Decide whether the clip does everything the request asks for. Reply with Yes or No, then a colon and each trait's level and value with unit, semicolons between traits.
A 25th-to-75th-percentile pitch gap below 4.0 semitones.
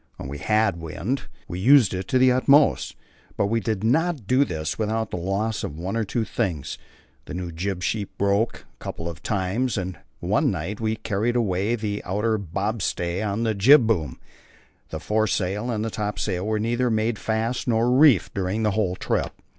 Yes: average, 3.6 semitones